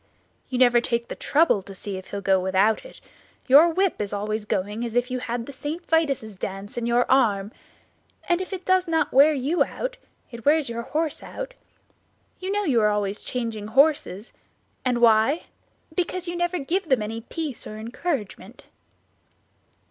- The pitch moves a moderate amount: No, wide, 7.1 semitones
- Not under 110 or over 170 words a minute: No, average, 185 wpm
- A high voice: Yes, high, 245 Hz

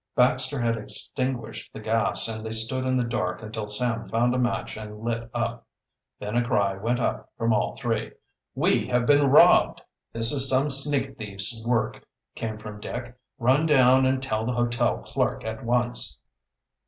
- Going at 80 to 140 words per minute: No, average, 175 wpm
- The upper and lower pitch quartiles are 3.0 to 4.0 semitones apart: No, narrow, 2.6 semitones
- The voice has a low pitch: Yes, low, 120 Hz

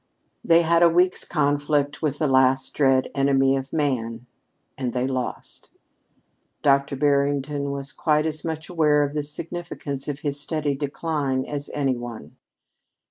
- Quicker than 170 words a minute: No, average, 145 wpm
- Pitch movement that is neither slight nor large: No, narrow, 2.1 semitones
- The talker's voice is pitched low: No, medium, 145 Hz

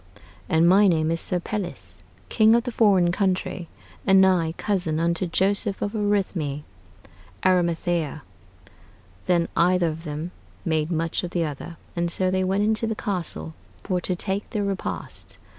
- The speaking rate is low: No, average, 155 wpm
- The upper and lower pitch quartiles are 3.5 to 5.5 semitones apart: No, average, 3.0 semitones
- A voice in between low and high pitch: Yes, medium, 180 Hz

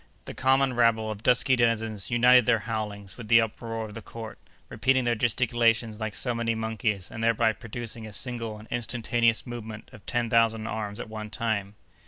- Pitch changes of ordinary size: No, narrow, 1.6 semitones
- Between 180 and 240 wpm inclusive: Yes, average, 185 wpm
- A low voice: Yes, low, 115 Hz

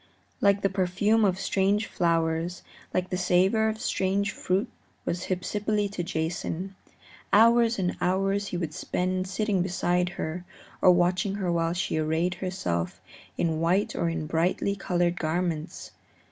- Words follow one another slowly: No, average, 145 wpm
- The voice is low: No, medium, 180 Hz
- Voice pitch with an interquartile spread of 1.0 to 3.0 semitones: Yes, narrow, 2.6 semitones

